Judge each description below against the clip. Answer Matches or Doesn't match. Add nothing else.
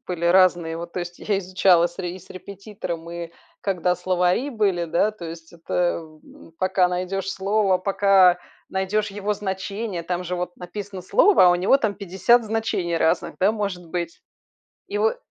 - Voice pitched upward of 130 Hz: Matches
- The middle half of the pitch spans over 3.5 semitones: Doesn't match